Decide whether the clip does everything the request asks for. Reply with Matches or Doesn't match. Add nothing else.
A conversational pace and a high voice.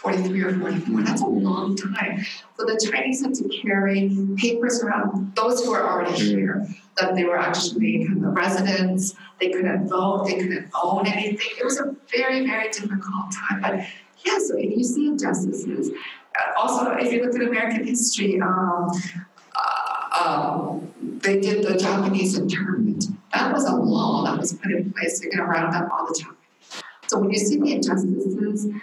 Matches